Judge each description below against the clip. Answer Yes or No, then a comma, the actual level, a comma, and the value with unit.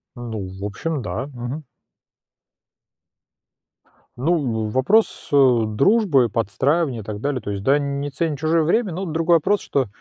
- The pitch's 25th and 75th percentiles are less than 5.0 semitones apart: No, wide, 5.6 semitones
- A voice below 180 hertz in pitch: Yes, medium, 140 Hz